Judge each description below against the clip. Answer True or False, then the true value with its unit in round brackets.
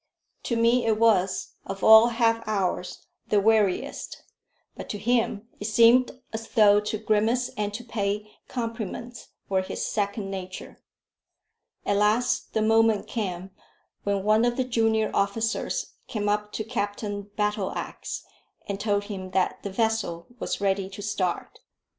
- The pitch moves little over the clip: True (2.1 semitones)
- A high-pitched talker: True (210 Hz)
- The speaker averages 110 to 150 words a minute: True (145 wpm)